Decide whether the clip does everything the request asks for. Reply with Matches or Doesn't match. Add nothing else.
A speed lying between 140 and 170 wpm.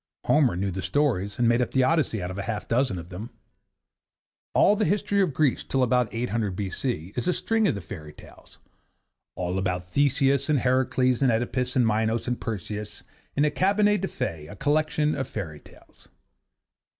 Doesn't match